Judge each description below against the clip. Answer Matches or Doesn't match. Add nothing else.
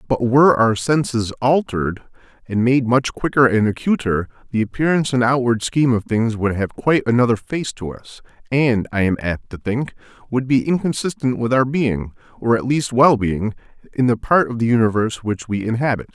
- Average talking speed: Matches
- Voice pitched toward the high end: Doesn't match